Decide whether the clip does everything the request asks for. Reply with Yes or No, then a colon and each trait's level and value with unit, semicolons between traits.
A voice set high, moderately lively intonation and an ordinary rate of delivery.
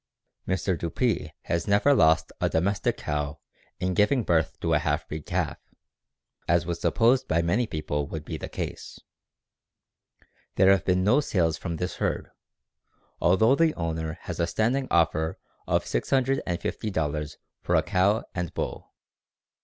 No: very low, 85 Hz; average, 4.5 semitones; average, 145 wpm